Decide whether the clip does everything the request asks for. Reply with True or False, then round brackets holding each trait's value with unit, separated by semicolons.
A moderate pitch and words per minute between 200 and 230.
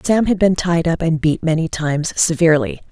True (165 Hz; 205 wpm)